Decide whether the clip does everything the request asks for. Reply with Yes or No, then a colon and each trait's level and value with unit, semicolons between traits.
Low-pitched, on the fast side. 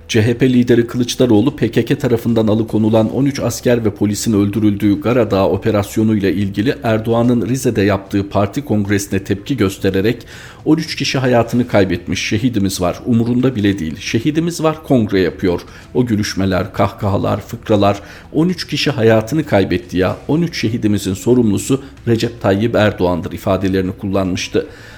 No: low, 110 Hz; average, 125 wpm